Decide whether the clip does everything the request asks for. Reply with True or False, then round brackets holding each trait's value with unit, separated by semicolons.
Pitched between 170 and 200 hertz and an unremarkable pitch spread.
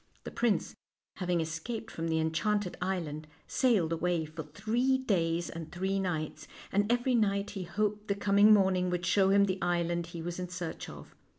True (185 Hz; 3.5 semitones)